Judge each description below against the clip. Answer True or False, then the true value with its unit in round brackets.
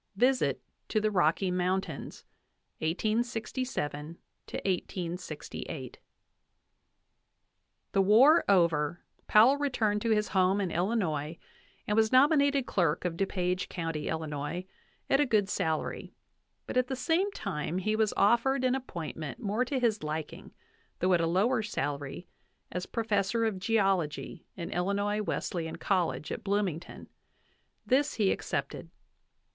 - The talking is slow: True (125 wpm)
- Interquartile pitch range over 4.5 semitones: True (5.2 semitones)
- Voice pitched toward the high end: True (195 Hz)